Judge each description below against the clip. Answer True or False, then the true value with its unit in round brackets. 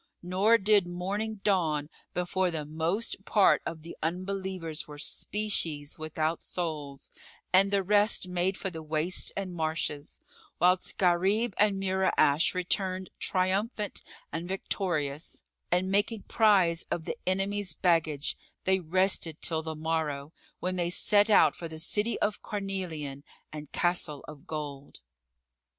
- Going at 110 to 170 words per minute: True (135 wpm)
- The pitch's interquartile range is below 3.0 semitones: False (3.6 semitones)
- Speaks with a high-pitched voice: False (180 Hz)